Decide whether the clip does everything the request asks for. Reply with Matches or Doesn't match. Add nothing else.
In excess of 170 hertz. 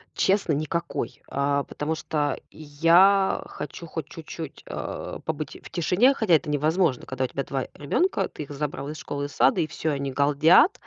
Doesn't match